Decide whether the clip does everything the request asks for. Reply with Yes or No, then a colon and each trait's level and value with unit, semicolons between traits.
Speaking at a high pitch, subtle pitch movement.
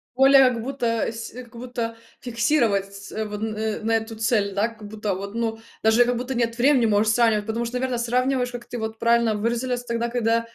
Yes: high, 230 Hz; narrow, 1.9 semitones